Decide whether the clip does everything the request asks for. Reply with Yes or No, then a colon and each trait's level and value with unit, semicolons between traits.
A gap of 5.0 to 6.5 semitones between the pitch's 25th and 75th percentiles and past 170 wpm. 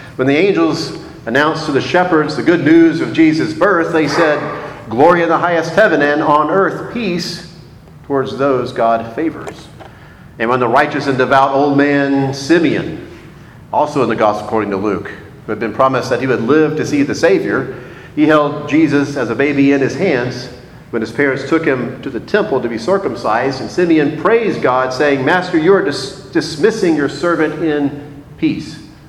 No: average, 3.1 semitones; average, 185 wpm